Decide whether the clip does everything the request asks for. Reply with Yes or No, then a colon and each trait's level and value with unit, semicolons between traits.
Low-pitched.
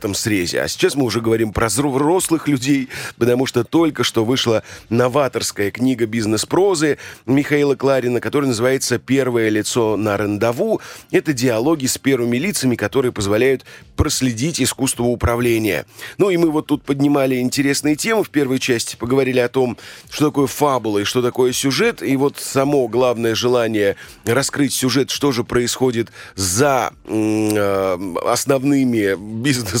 Yes: low, 125 Hz